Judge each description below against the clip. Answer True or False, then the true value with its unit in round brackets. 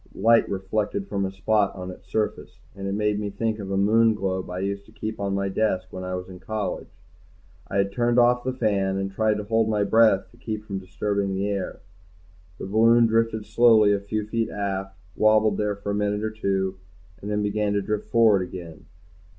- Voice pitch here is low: True (105 Hz)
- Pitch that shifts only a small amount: True (2.0 semitones)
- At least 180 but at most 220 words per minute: True (205 wpm)